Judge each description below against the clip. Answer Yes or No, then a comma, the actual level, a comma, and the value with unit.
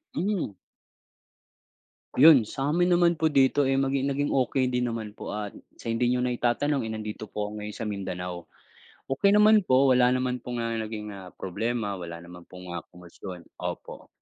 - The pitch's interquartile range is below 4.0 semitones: No, average, 4.7 semitones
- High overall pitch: No, low, 120 Hz